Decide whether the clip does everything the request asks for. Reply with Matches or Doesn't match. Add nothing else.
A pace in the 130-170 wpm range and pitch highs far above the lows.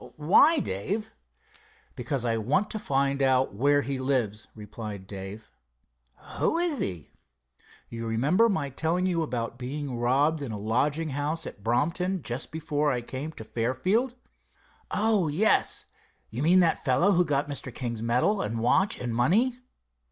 Matches